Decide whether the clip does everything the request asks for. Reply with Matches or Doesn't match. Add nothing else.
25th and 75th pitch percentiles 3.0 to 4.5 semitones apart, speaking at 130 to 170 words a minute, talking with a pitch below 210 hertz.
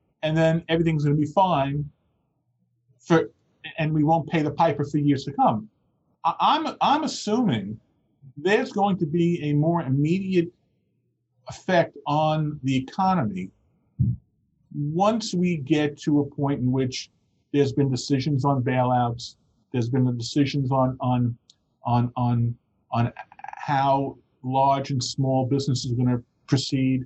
Matches